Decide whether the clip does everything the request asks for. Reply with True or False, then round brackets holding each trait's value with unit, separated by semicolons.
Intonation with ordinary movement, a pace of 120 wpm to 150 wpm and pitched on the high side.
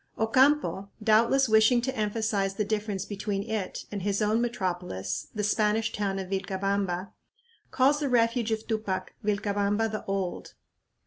False (2.2 semitones; 140 wpm; 210 Hz)